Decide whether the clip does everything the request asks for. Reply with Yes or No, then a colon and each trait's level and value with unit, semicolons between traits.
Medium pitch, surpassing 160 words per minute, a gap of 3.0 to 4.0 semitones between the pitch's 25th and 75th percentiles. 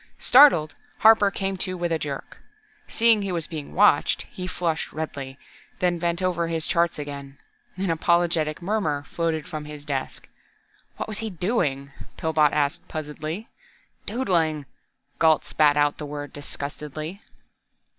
No: medium, 160 Hz; average, 140 wpm; average, 3.6 semitones